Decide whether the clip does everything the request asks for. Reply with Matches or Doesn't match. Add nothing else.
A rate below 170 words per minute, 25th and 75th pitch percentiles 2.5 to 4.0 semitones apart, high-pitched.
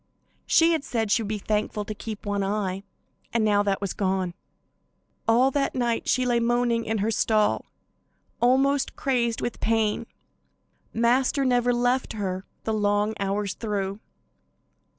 Matches